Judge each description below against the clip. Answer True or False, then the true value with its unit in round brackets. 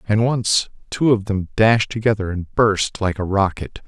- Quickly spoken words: False (185 wpm)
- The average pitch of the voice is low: True (105 Hz)